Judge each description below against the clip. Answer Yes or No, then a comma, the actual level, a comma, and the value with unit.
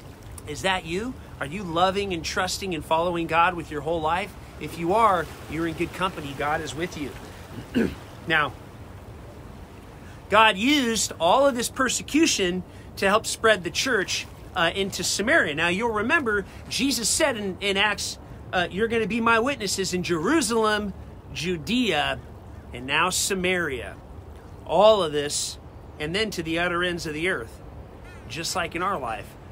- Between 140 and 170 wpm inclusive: Yes, average, 160 wpm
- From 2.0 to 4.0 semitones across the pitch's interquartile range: No, average, 5.3 semitones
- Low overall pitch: No, medium, 180 Hz